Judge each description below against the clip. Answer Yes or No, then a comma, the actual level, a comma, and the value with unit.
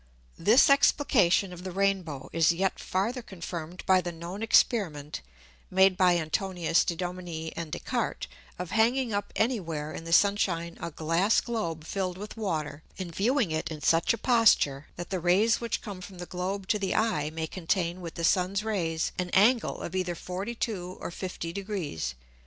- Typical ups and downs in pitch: Yes, average, 3.5 semitones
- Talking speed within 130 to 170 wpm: No, average, 185 wpm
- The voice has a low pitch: No, medium, 180 Hz